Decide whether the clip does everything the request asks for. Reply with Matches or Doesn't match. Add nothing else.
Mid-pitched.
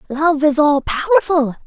Doesn't match